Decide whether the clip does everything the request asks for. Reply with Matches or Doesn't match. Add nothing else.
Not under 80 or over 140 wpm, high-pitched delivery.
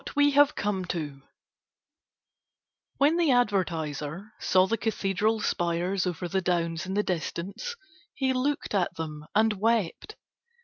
Matches